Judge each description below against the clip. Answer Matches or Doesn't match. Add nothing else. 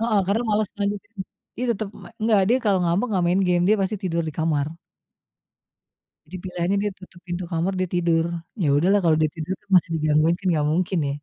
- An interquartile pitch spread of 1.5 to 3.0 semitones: Doesn't match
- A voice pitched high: Doesn't match